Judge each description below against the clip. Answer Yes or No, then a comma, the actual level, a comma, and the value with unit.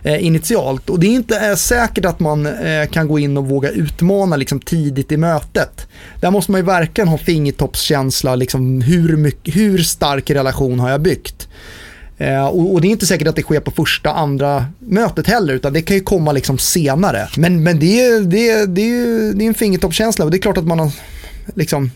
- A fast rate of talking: Yes, fast, 210 wpm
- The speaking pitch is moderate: Yes, medium, 160 Hz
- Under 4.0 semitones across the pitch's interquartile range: No, wide, 5.5 semitones